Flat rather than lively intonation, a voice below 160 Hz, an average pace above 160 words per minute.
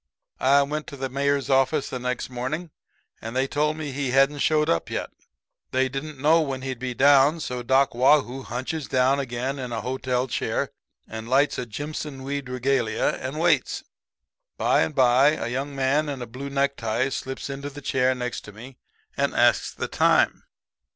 Yes: narrow, 2.0 semitones; low, 135 Hz; average, 185 wpm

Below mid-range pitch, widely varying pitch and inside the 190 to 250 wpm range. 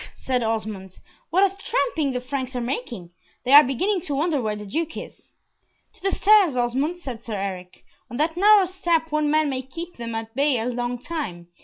No: very high, 265 Hz; wide, 6.0 semitones; average, 200 wpm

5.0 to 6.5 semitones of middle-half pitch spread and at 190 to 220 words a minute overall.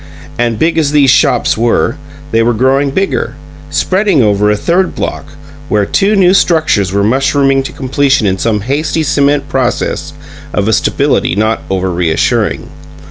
No: wide, 5.5 semitones; average, 155 wpm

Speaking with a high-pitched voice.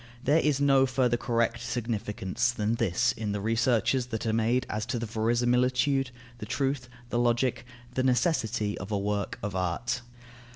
No: low, 120 Hz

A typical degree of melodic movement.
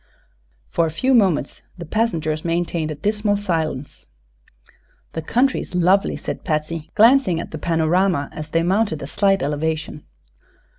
Yes: average, 4.3 semitones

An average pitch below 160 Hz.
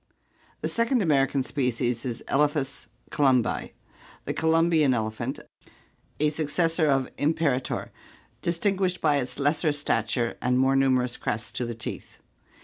Yes: medium, 140 Hz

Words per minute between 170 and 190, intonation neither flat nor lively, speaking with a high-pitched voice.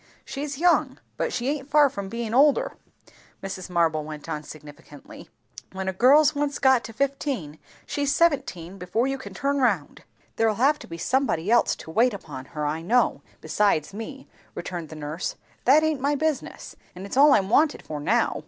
No: average, 180 wpm; wide, 8.8 semitones; high, 230 Hz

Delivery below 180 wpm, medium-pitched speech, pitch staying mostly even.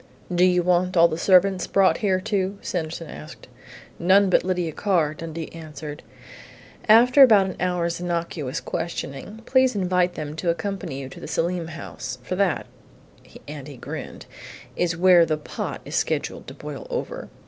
No: average, 170 wpm; medium, 175 Hz; average, 3.0 semitones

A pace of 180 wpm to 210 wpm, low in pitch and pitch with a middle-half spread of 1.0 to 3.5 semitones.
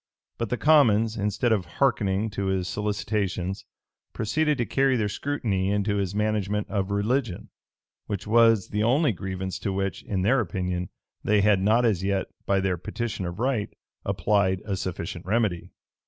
No: average, 160 wpm; low, 105 Hz; average, 2.9 semitones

